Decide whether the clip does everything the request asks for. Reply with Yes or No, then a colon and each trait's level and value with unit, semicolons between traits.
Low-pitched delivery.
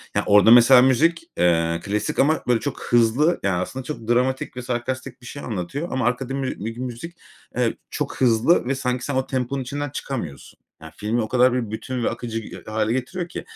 Yes: low, 125 Hz